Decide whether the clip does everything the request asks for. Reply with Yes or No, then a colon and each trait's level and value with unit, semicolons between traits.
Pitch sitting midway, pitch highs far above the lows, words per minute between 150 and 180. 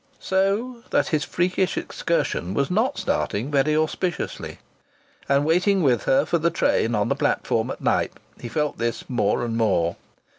Yes: medium, 150 Hz; wide, 7.4 semitones; average, 160 wpm